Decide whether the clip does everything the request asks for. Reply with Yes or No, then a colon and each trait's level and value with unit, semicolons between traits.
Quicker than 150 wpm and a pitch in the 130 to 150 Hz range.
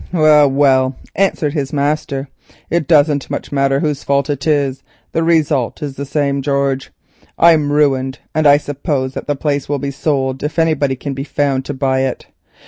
Yes: average, 180 wpm; medium, 140 Hz